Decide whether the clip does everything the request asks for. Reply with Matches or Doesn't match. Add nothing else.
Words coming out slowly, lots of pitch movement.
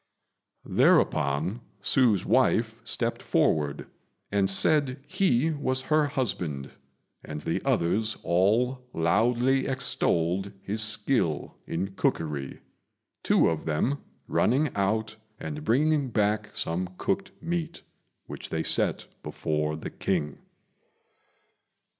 Matches